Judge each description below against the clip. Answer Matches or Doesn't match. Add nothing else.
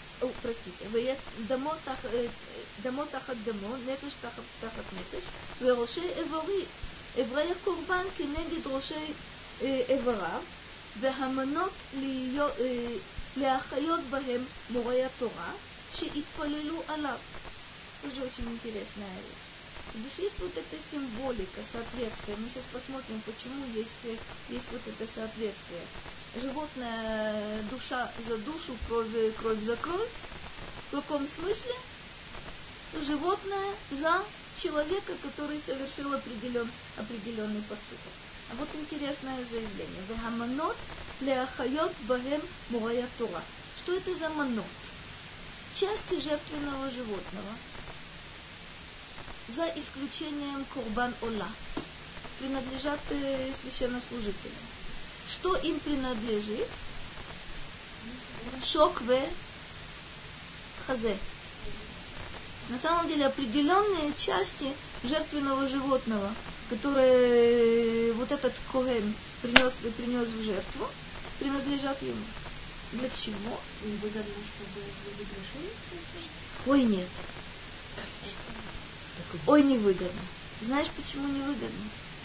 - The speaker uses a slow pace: Matches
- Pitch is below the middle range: Doesn't match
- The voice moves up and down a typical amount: Matches